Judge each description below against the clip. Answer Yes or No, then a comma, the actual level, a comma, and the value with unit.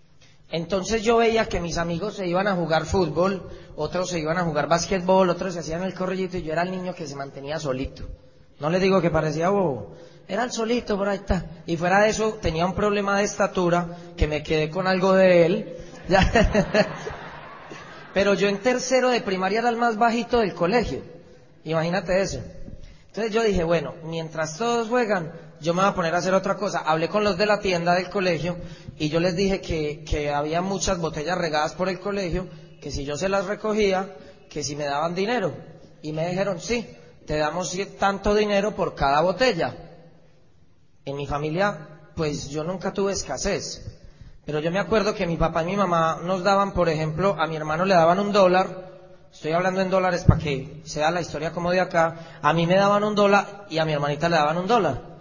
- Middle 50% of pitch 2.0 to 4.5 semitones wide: Yes, average, 3.5 semitones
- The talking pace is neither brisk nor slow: No, fast, 205 wpm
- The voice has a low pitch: No, medium, 180 Hz